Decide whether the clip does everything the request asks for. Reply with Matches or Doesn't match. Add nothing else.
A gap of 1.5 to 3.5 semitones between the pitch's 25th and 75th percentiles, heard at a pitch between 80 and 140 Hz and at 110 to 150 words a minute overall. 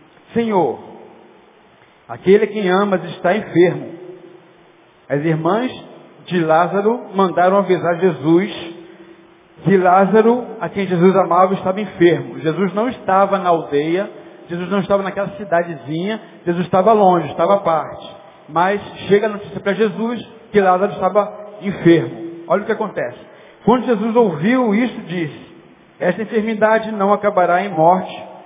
Doesn't match